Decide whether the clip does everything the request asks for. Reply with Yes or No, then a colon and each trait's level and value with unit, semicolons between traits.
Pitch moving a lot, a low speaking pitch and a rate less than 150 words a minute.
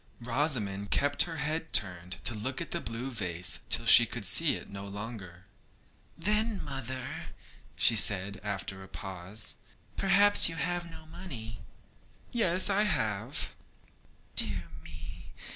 Yes: wide, 8.7 semitones; low, 115 Hz; slow, 135 wpm